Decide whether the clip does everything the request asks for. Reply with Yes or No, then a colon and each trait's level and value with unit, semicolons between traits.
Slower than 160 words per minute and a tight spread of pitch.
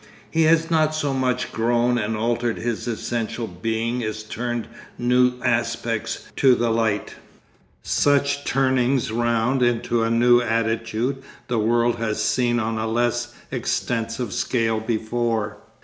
Yes: slow, 135 wpm; narrow, 1.6 semitones